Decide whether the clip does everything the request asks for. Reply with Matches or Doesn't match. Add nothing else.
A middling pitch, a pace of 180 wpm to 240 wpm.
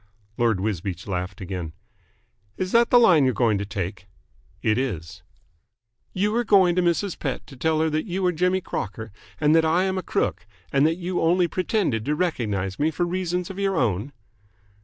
Matches